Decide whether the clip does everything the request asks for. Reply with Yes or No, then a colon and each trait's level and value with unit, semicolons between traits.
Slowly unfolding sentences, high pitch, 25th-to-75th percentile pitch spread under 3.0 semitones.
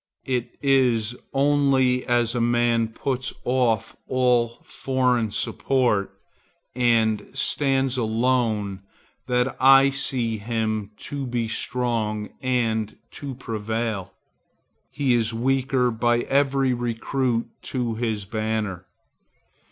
No: slow, 100 wpm; low, 120 Hz; narrow, 2.6 semitones